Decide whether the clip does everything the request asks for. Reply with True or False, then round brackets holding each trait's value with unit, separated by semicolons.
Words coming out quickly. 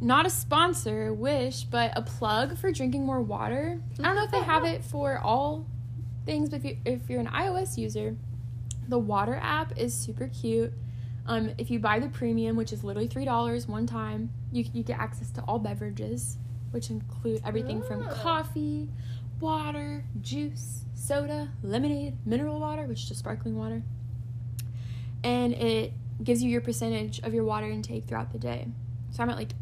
False (175 wpm)